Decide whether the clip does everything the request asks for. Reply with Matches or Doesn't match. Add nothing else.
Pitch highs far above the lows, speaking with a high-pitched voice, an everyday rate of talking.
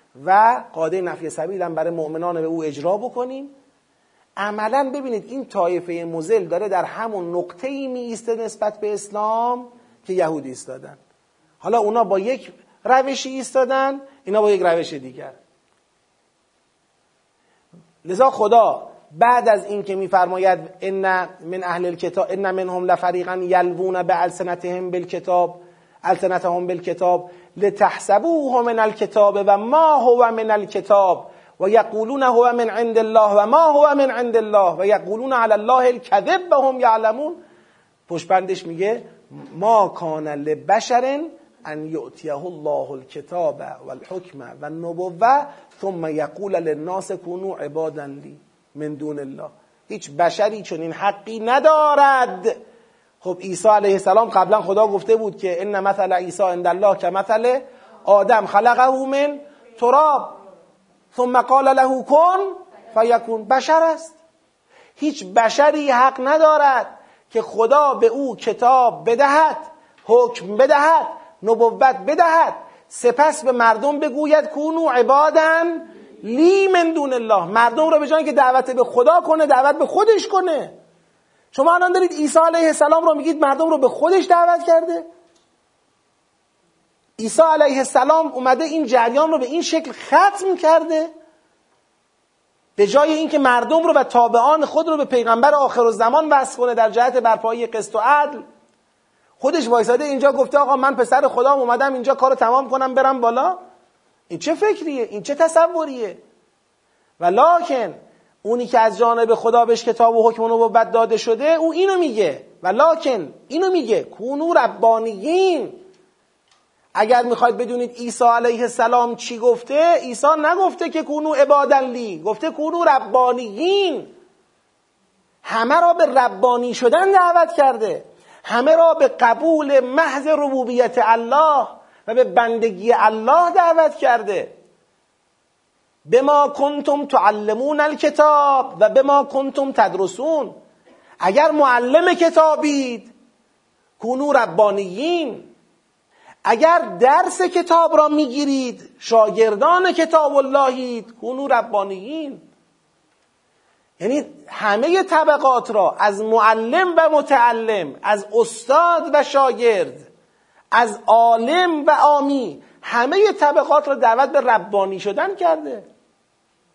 Matches